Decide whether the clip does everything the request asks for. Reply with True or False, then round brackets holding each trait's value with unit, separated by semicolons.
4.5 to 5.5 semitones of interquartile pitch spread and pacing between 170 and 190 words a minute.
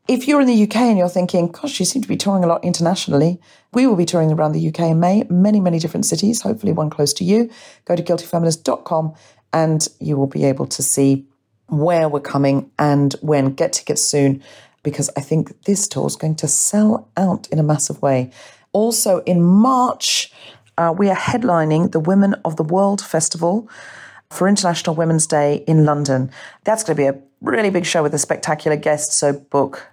False (4.8 semitones; 200 wpm)